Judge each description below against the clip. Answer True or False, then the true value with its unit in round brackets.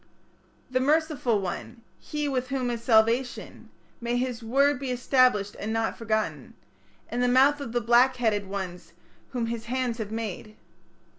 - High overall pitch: True (240 Hz)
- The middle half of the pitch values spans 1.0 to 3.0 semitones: True (2.6 semitones)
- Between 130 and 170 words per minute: True (155 wpm)